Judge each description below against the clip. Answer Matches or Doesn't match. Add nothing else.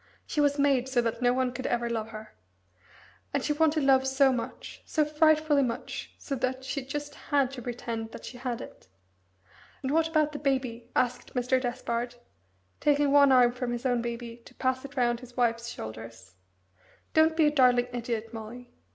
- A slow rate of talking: Doesn't match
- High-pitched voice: Matches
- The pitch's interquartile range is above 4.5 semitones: Doesn't match